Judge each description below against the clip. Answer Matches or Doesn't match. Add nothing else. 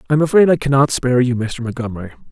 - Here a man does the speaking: Matches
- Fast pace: Matches